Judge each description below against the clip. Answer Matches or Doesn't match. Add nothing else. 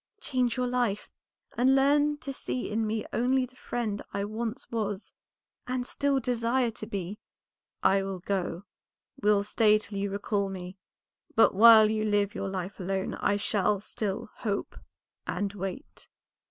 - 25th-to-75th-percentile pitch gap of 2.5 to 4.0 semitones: Matches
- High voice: Matches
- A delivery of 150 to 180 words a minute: Matches